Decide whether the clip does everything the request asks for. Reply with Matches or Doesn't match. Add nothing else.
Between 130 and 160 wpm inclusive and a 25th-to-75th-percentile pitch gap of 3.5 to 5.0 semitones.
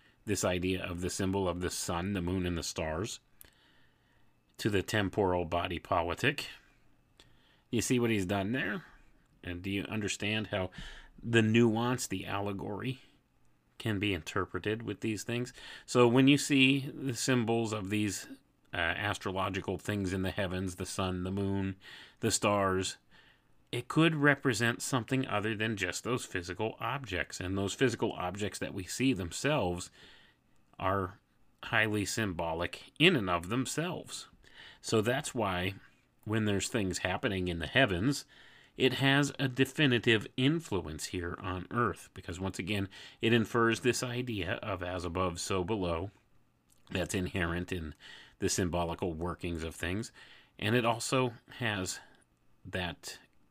Matches